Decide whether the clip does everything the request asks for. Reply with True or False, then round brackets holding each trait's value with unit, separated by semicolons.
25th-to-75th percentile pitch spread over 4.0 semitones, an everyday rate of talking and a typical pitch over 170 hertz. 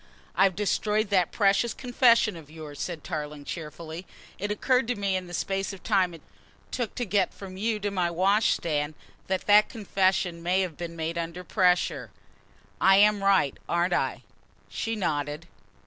False (3.5 semitones; 170 wpm; 185 Hz)